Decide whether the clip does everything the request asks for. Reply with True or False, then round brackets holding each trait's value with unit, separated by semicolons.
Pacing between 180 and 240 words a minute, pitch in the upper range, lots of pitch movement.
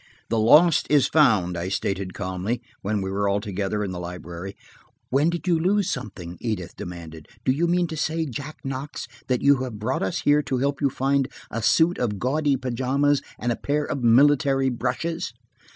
False (185 wpm; 125 Hz; 6.5 semitones)